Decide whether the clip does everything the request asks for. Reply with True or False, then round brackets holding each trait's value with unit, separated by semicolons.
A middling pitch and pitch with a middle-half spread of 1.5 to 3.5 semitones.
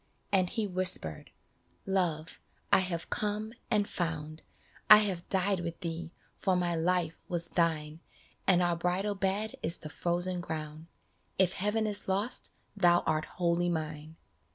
True (175 Hz; 2.9 semitones)